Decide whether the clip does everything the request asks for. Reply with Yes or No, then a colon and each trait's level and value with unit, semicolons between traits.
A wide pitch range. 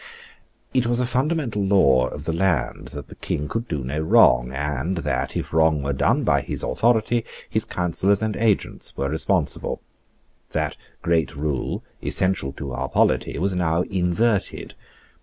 Yes: wide, 6.5 semitones